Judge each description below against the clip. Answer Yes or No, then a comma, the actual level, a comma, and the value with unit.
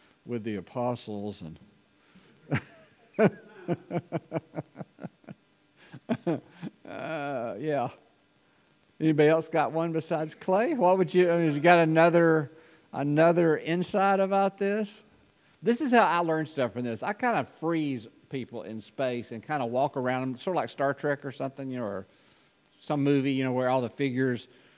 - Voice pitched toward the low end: No, medium, 145 Hz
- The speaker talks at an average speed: Yes, average, 155 wpm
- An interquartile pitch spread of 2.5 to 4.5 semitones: No, average, 5.0 semitones